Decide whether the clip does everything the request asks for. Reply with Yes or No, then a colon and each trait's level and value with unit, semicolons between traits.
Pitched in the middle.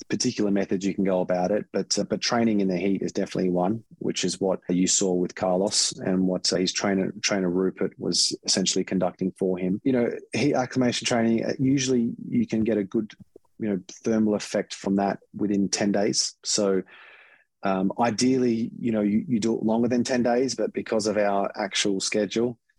No: low, 105 Hz